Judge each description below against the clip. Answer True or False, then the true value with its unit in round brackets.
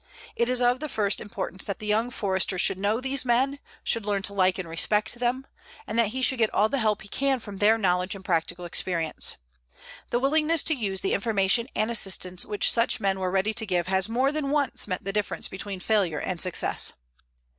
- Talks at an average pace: False (215 wpm)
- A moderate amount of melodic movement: True (4.2 semitones)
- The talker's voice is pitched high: True (210 Hz)